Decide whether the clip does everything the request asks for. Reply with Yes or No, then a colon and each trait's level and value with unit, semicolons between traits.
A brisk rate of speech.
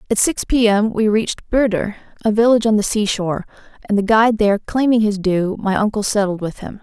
Yes: fast, 210 wpm